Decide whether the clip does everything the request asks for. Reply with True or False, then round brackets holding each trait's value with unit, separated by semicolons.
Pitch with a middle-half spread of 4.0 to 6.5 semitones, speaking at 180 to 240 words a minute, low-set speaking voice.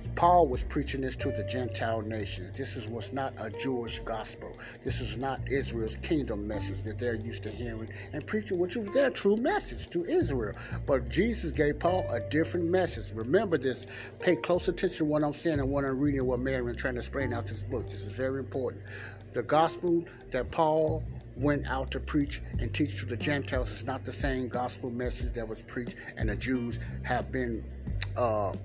True (5.1 semitones; 200 wpm; 125 Hz)